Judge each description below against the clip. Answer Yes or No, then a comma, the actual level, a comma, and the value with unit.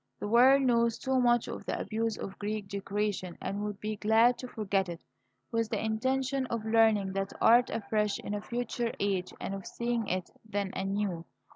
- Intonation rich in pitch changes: No, average, 2.9 semitones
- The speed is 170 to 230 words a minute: Yes, average, 185 wpm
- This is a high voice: Yes, high, 215 Hz